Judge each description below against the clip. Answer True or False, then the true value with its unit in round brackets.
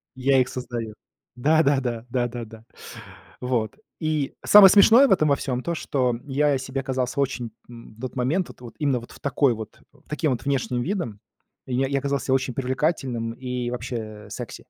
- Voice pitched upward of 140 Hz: False (130 Hz)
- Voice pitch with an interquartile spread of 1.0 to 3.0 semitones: True (2.6 semitones)